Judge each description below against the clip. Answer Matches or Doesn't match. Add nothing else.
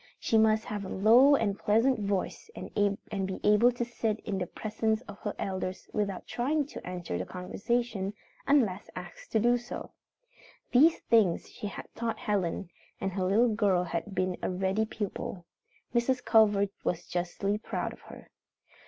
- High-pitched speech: Matches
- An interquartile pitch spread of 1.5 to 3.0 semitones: Doesn't match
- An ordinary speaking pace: Matches